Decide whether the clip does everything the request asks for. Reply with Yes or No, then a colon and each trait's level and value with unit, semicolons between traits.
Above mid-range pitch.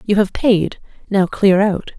Yes: high, 195 Hz